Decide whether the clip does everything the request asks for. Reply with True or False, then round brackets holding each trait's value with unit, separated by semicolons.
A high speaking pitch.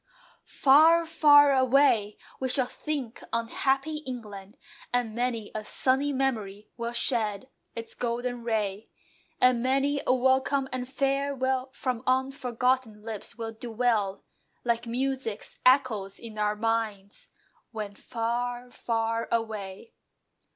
True (245 Hz)